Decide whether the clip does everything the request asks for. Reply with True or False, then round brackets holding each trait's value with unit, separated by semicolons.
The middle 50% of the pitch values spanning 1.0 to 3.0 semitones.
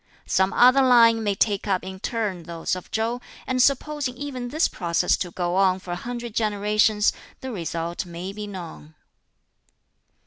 False (4.9 semitones)